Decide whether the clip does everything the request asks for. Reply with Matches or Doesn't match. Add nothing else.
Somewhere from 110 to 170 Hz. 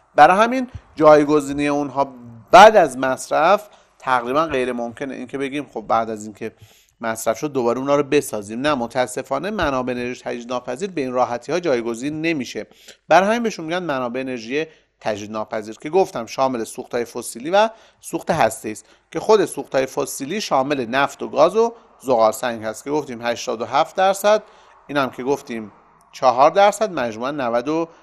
Matches